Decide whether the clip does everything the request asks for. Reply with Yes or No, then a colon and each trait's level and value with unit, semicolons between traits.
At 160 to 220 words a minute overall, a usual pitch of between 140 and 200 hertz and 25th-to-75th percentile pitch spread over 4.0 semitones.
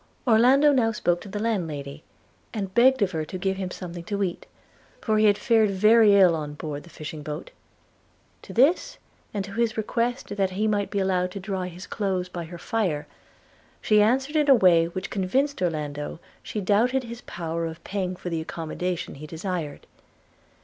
Yes: average, 185 wpm; high, 190 Hz; average, 4.4 semitones